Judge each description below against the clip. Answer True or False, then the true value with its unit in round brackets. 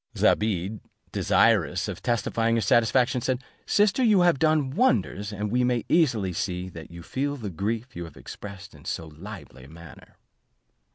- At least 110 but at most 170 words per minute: True (165 wpm)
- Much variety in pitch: True (6.2 semitones)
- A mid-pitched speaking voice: False (110 Hz)